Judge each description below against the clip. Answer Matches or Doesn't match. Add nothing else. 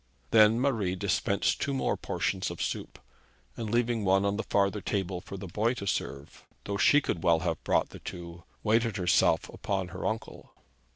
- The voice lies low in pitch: Matches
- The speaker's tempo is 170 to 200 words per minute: Matches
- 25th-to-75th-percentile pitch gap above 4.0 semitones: Doesn't match